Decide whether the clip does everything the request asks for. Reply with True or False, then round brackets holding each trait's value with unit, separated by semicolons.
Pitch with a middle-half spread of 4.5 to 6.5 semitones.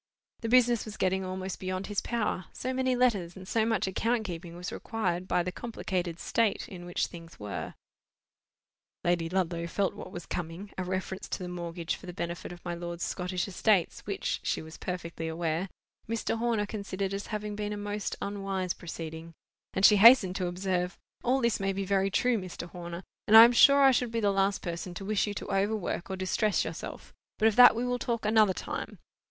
False (3.5 semitones)